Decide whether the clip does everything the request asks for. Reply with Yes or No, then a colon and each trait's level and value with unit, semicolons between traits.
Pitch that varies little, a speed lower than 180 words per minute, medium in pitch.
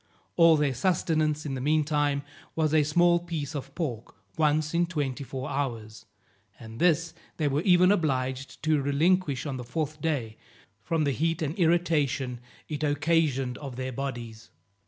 No: average, 3.5 semitones; average, 155 wpm; medium, 150 Hz